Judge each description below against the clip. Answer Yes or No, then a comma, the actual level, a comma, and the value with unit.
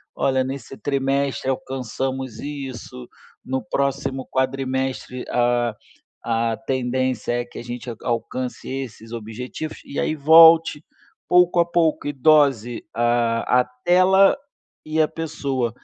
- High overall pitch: No, low, 130 Hz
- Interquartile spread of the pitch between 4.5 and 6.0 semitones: No, average, 3.1 semitones